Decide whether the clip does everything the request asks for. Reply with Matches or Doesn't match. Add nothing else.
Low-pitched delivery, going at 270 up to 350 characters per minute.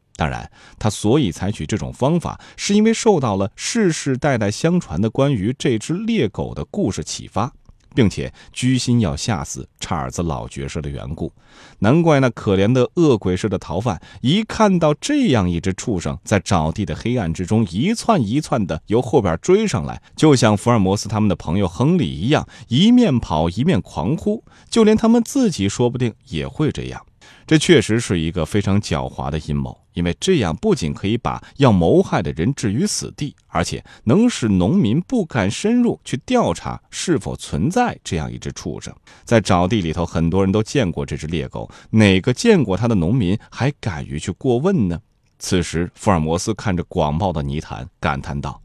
Matches